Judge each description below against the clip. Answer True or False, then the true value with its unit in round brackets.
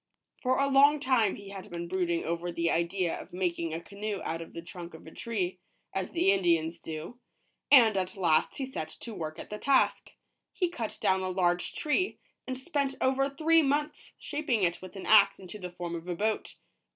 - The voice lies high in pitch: True (195 Hz)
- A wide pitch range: True (7.2 semitones)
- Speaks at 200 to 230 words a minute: True (205 wpm)